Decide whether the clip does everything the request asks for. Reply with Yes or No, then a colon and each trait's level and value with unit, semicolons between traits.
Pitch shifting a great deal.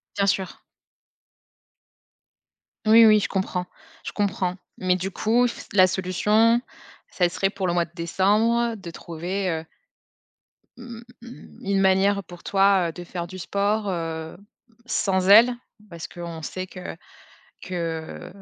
No: average, 2.7 semitones